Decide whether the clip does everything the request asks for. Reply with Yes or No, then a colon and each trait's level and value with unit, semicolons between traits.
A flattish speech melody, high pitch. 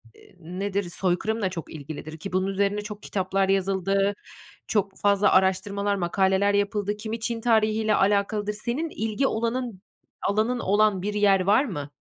Yes: narrow, 2.1 semitones; high, 200 Hz